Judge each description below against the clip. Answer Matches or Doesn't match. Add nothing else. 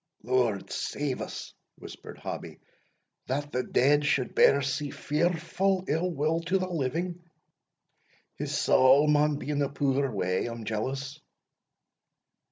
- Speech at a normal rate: Doesn't match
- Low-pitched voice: Doesn't match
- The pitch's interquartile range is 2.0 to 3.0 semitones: Doesn't match